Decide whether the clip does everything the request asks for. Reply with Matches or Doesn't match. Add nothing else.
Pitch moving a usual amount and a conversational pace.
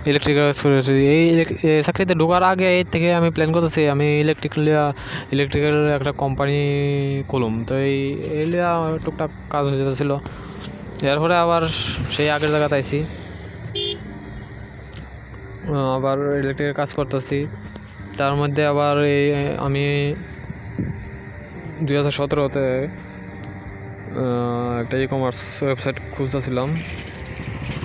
Doesn't match